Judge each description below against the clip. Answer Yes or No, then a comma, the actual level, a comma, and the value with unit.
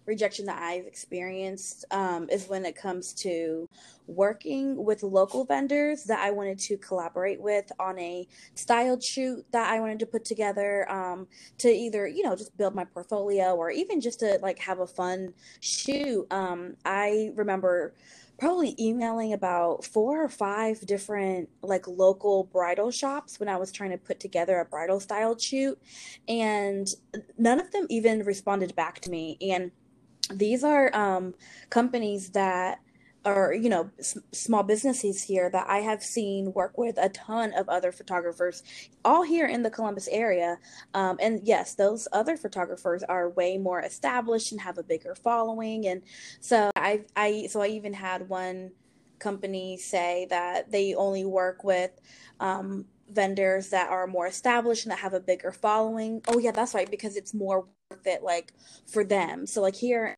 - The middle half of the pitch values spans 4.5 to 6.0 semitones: No, average, 3.2 semitones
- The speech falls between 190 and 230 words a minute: No, average, 170 wpm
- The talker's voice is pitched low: No, high, 200 Hz